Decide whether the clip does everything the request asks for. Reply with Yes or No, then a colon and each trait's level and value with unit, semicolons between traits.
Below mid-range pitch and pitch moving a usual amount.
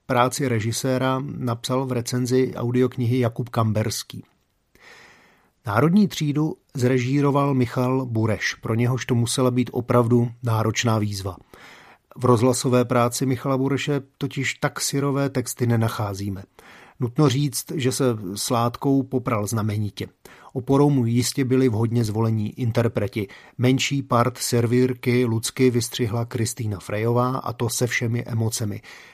No: low, 125 Hz; narrow, 2.2 semitones